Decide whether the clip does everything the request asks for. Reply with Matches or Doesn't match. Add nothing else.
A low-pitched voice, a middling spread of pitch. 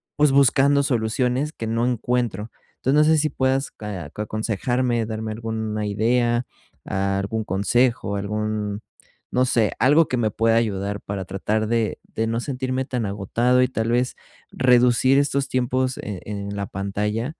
Matches